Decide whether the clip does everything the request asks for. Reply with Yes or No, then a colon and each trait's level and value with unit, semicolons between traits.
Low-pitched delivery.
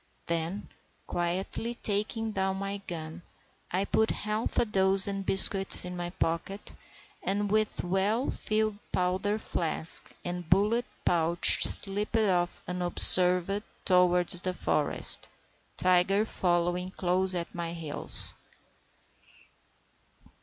No: medium, 185 Hz